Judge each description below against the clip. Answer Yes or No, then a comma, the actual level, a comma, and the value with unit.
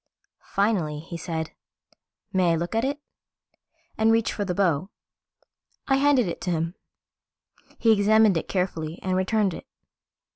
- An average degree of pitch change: Yes, average, 4.7 semitones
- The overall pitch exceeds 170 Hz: Yes, high, 190 Hz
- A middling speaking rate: Yes, average, 145 wpm